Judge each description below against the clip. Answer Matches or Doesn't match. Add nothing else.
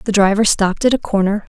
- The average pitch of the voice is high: Matches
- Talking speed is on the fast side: Matches